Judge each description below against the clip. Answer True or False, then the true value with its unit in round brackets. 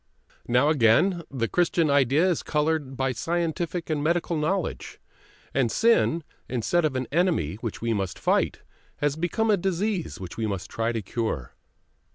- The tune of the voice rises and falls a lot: True (6.8 semitones)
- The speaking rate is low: False (160 wpm)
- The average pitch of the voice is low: False (150 Hz)